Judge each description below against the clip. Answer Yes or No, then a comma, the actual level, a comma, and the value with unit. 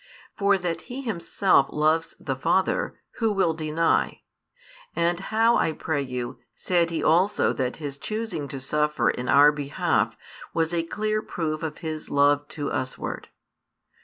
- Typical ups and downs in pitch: Yes, average, 4.5 semitones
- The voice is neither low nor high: Yes, medium, 160 Hz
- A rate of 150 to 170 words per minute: Yes, average, 155 wpm